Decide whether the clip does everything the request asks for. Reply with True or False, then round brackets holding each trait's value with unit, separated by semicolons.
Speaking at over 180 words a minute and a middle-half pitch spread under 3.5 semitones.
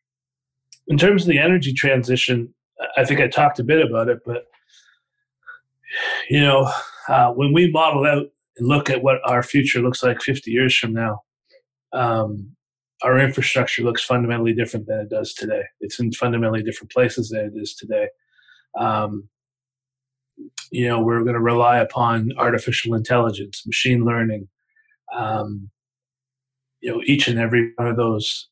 False (155 wpm; 2.8 semitones)